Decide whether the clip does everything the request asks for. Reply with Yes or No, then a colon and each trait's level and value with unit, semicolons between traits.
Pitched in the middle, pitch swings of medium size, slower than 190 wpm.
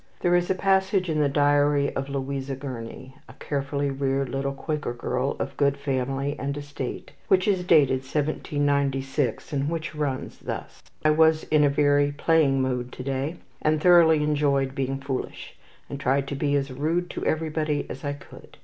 No: medium, 145 Hz; narrow, 2.1 semitones; average, 175 wpm